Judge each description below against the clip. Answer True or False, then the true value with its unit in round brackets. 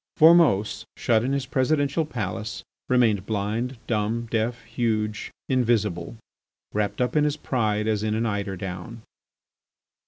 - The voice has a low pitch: True (115 Hz)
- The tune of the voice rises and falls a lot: False (3.2 semitones)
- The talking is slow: True (130 wpm)